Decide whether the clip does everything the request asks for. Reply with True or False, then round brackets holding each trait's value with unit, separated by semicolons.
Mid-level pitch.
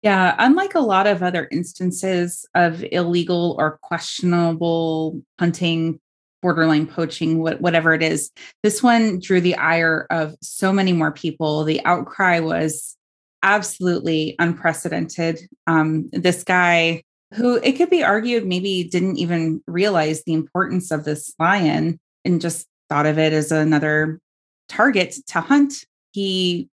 True (170 Hz)